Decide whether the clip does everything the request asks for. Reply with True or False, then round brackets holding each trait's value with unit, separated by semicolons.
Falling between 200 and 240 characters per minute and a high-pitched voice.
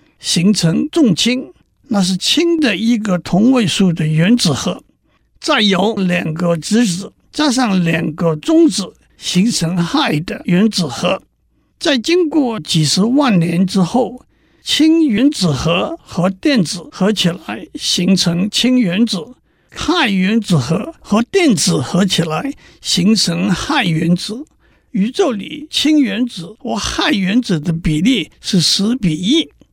False (190 characters per minute; 205 Hz)